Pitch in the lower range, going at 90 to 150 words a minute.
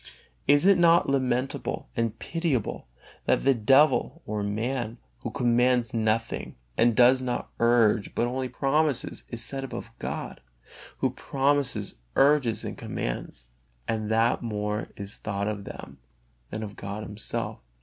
Yes: low, 120 Hz; average, 140 wpm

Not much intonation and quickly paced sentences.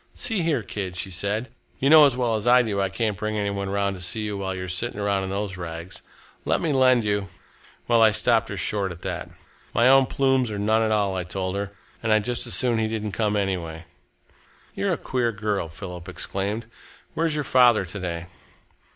No: average, 3.5 semitones; fast, 225 wpm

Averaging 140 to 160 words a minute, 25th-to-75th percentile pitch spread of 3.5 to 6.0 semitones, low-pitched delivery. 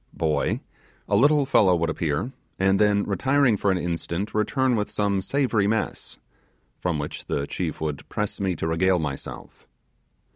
Yes: average, 155 wpm; average, 4.3 semitones; very low, 95 Hz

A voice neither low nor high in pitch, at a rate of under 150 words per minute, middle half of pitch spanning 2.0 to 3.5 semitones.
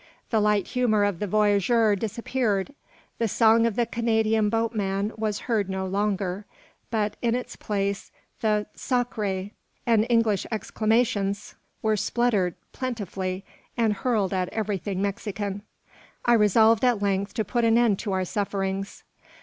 No: high, 210 Hz; average, 140 wpm; narrow, 2.5 semitones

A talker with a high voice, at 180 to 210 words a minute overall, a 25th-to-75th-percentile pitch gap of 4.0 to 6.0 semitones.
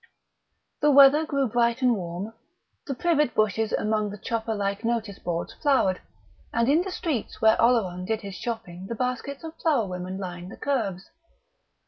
No: high, 225 Hz; average, 165 wpm; wide, 5.5 semitones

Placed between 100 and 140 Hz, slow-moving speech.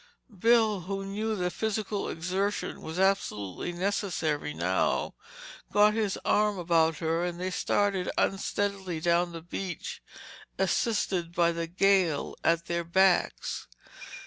No: medium, 185 Hz; slow, 120 wpm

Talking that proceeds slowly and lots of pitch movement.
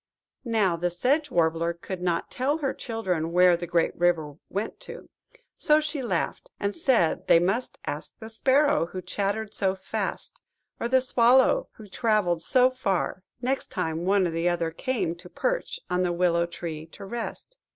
No: average, 170 wpm; wide, 6.5 semitones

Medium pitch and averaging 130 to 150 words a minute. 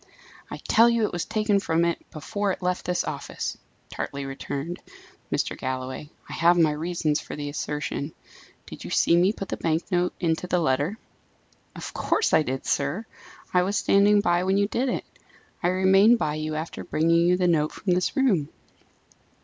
No: medium, 175 Hz; average, 185 wpm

